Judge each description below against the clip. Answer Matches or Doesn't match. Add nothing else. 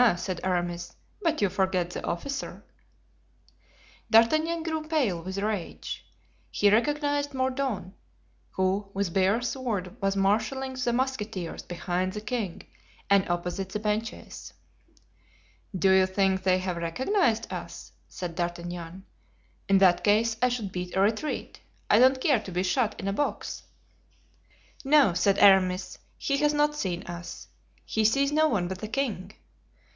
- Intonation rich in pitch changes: Matches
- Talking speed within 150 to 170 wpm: Doesn't match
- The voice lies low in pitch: Doesn't match